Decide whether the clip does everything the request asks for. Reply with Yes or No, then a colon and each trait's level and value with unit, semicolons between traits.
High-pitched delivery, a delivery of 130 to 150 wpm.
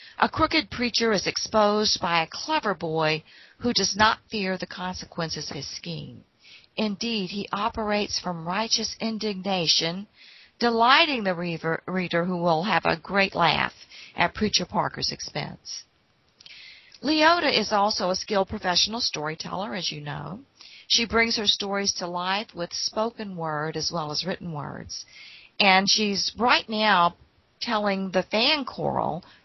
Yes: high, 195 Hz; average, 140 wpm